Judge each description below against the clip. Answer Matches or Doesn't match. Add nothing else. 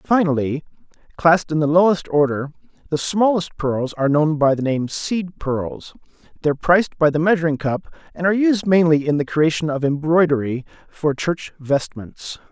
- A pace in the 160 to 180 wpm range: Matches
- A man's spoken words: Matches